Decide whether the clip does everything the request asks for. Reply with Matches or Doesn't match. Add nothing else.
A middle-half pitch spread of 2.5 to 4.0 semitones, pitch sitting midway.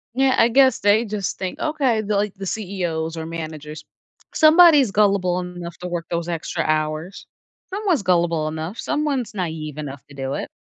Doesn't match